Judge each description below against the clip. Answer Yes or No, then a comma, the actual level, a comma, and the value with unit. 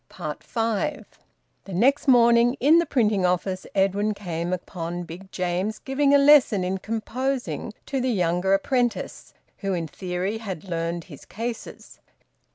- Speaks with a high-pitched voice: Yes, high, 205 Hz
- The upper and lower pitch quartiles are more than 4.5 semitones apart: Yes, average, 5.2 semitones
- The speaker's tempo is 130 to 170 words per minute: Yes, average, 140 wpm